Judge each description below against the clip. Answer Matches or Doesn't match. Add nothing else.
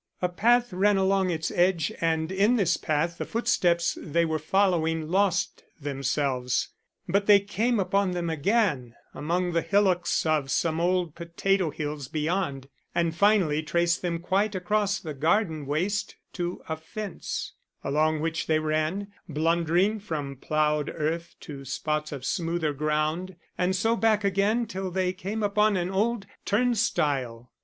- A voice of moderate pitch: Matches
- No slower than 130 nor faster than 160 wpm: Matches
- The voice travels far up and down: Doesn't match